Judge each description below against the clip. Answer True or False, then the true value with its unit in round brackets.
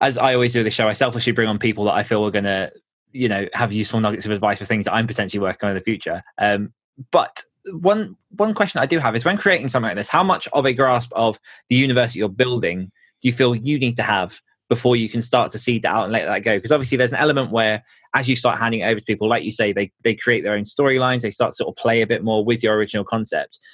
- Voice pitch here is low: True (115 Hz)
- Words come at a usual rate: False (290 wpm)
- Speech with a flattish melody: False (3.3 semitones)